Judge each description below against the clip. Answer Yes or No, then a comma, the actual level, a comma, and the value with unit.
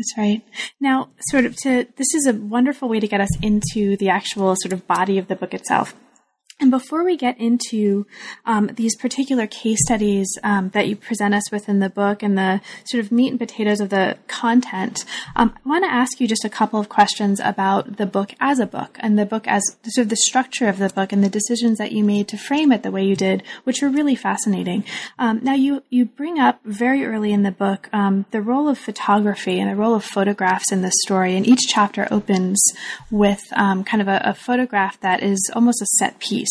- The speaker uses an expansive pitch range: No, average, 3.5 semitones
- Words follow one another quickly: Yes, fast, 230 wpm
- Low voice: No, high, 210 Hz